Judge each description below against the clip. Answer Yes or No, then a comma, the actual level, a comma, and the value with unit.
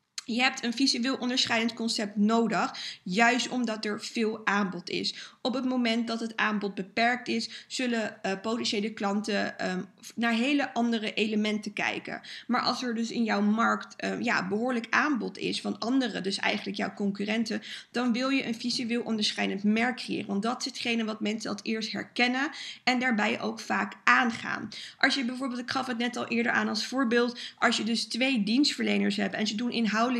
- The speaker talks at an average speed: Yes, average, 185 wpm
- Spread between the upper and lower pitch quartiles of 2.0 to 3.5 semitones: Yes, narrow, 2.6 semitones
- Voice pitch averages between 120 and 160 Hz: No, high, 230 Hz